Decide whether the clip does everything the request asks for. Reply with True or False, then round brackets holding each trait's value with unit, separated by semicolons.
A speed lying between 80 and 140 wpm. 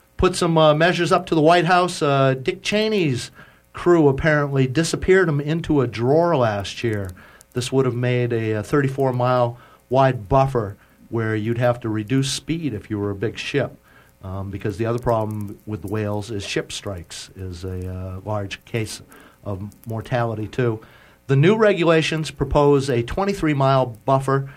False (160 wpm)